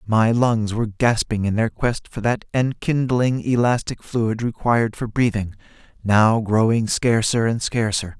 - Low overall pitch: Yes, low, 115 Hz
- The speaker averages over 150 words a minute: No, average, 145 wpm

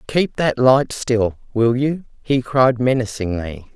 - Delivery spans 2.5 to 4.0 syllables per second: Yes, 3.7 syllables/s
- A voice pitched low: Yes, low, 125 Hz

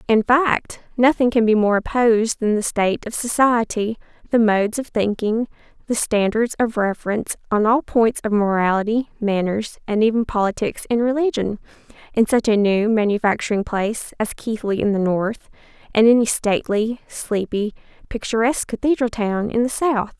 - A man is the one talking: No, female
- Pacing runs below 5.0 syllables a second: No, 5.1 syllables/s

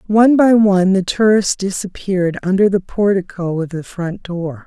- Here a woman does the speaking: Yes, female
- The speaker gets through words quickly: No, average, 165 wpm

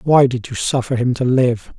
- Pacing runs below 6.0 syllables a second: Yes, 4.8 syllables/s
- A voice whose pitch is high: No, low, 125 Hz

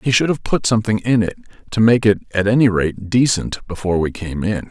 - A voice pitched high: No, low, 105 Hz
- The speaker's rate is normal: No, fast, 230 wpm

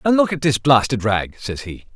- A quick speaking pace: Yes, fast, 245 wpm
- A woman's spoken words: No, male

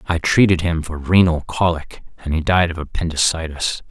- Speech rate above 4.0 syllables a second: Yes, 5.2 syllables/s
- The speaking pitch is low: Yes, very low, 85 Hz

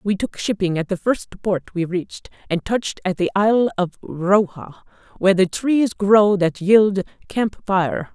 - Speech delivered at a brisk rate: No, average, 170 wpm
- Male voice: No, female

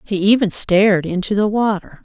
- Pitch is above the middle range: Yes, high, 200 Hz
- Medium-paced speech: Yes, average, 175 wpm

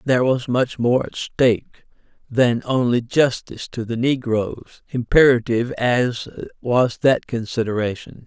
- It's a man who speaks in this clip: Yes, male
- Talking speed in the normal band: No, slow, 125 wpm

